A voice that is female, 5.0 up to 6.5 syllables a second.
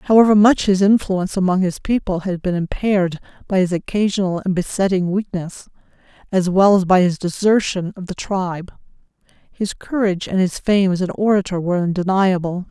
Yes: female; 5.5 syllables/s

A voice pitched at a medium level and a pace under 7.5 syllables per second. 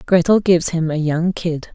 Yes: medium, 170 Hz; 5.0 syllables/s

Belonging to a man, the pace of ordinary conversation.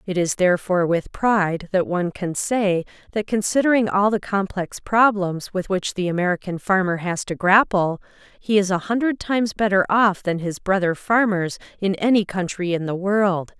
No: female; average, 175 wpm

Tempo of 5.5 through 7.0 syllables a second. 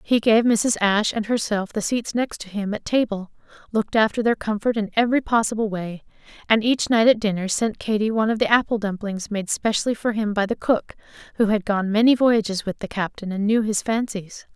Yes: 5.6 syllables/s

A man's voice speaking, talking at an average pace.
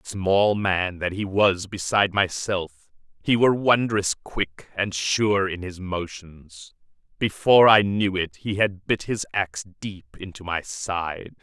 Yes: male; average, 150 wpm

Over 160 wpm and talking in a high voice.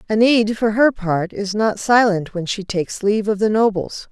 Yes: fast, 205 wpm; high, 210 Hz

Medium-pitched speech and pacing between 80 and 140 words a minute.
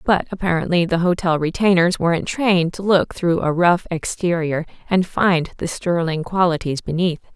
No: medium, 175 Hz; average, 155 wpm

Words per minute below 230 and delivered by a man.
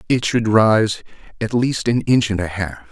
Yes: fast, 205 wpm; male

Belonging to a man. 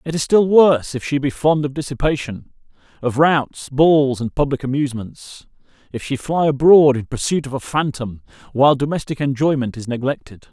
Yes: male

